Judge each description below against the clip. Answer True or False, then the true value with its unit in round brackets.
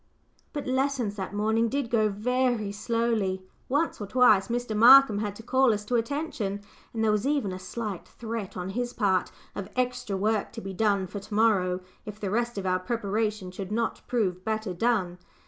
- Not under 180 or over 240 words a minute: True (190 wpm)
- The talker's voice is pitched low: False (215 Hz)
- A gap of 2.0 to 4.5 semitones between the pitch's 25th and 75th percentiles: True (3.3 semitones)